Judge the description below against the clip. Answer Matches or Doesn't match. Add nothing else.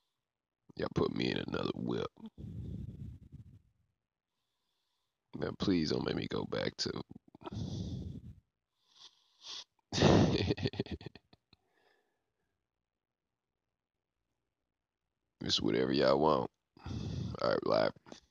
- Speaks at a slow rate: Matches